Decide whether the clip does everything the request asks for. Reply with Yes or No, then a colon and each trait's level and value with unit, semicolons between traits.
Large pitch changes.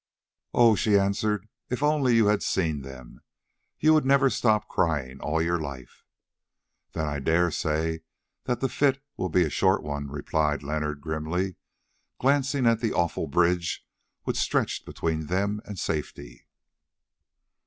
Yes: wide, 6.7 semitones